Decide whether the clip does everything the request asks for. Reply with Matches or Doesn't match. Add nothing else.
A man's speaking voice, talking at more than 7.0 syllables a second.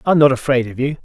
Matches